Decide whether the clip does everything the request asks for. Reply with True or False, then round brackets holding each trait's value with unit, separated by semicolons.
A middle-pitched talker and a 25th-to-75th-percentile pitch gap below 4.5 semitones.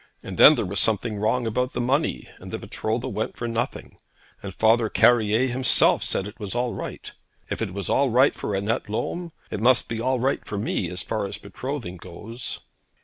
False (115 Hz; 3.4 semitones)